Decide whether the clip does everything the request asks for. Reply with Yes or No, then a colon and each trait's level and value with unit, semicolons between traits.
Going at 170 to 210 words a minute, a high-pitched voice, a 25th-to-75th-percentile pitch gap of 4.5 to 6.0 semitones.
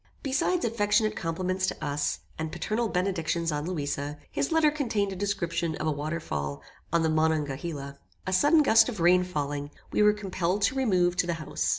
No: average, 180 wpm; medium, 175 Hz; average, 5.2 semitones